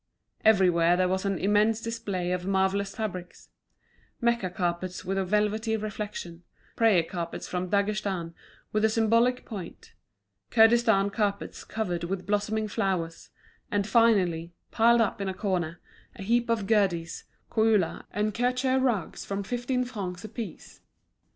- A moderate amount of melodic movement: Yes, average, 3.4 semitones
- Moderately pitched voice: No, high, 200 Hz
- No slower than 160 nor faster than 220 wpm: No, average, 140 wpm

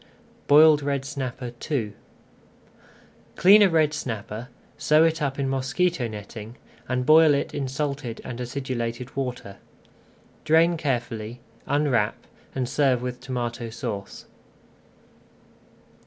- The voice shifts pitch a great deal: No, average, 3.7 semitones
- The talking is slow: Yes, slow, 110 wpm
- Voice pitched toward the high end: No, low, 130 Hz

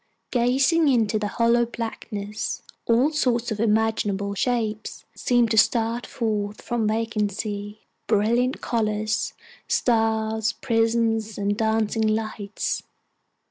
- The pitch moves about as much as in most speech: No, narrow, 1.8 semitones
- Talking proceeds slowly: Yes, slow, 100 wpm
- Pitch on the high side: Yes, high, 220 Hz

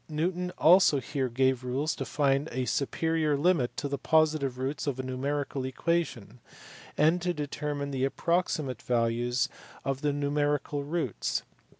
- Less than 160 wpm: Yes, average, 150 wpm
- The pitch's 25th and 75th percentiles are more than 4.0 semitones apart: No, average, 3.0 semitones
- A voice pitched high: No, medium, 140 Hz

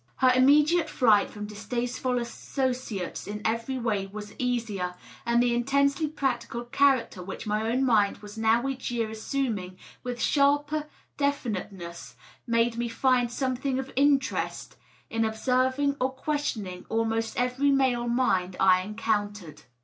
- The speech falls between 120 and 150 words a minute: Yes, slow, 135 wpm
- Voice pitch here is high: Yes, high, 240 Hz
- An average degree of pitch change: Yes, average, 3.8 semitones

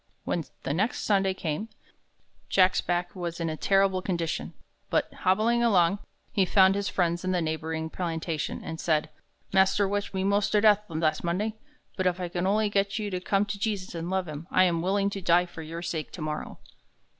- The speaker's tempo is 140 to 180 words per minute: No, average, 195 wpm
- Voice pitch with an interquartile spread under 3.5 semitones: Yes, average, 3.1 semitones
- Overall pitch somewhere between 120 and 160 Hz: No, medium, 185 Hz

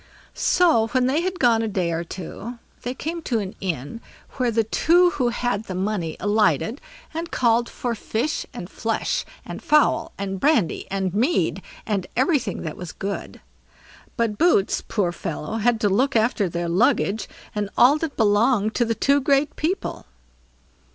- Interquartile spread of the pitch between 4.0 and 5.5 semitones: Yes, average, 5.2 semitones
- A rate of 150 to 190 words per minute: Yes, average, 165 wpm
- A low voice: No, high, 225 Hz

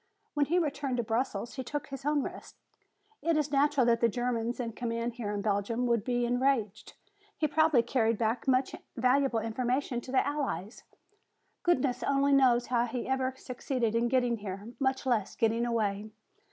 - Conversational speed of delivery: Yes, average, 175 wpm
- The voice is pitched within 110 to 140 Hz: No, high, 245 Hz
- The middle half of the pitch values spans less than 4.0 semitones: Yes, average, 2.9 semitones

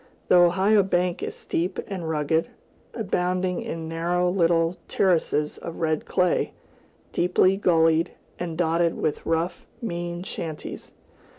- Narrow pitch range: Yes, narrow, 1.7 semitones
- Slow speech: Yes, slow, 120 wpm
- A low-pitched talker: No, medium, 175 Hz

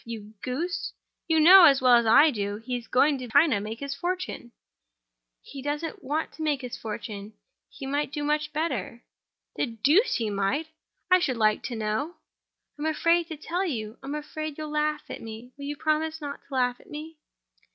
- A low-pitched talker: No, very high, 285 Hz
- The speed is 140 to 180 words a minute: No, average, 195 wpm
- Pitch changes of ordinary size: Yes, average, 4.8 semitones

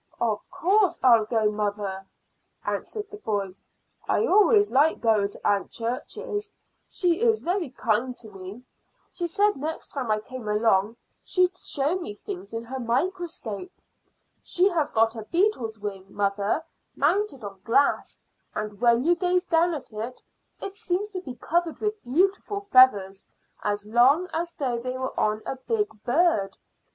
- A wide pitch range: Yes, wide, 8.8 semitones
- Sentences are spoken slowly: No, average, 155 wpm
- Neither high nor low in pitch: No, very high, 255 Hz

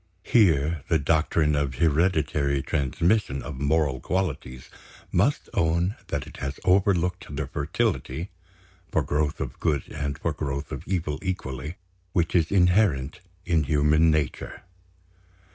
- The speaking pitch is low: Yes, very low, 75 Hz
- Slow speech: Yes, slow, 125 wpm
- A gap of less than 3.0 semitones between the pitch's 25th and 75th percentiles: No, average, 3.7 semitones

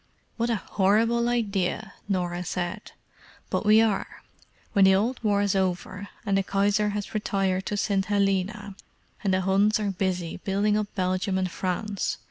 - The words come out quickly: No, average, 150 wpm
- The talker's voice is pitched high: Yes, high, 200 Hz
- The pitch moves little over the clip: Yes, narrow, 1.9 semitones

